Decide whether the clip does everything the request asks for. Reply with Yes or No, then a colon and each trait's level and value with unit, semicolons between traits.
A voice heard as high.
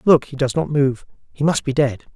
No: medium, 140 Hz